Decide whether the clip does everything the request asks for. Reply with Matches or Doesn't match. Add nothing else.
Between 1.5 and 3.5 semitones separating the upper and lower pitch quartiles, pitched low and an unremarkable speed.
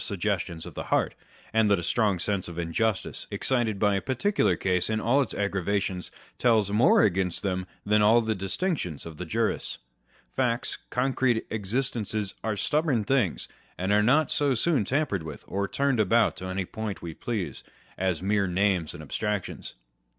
Doesn't match